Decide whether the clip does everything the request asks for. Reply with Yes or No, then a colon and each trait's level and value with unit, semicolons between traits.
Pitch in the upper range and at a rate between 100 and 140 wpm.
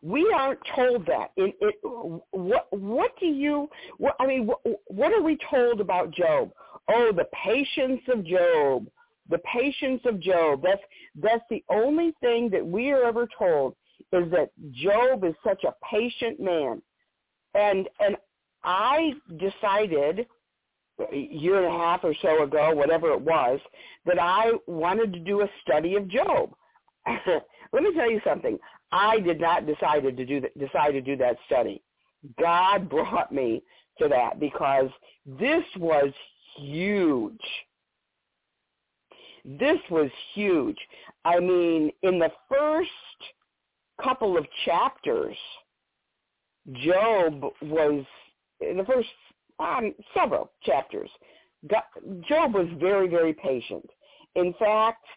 Yes: high, 215 Hz; slow, 135 wpm